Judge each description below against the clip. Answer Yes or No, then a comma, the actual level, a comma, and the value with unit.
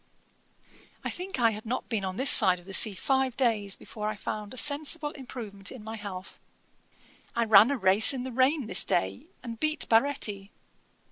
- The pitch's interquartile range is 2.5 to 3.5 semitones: No, average, 4.7 semitones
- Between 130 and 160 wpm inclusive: No, average, 190 wpm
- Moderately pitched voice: No, high, 225 Hz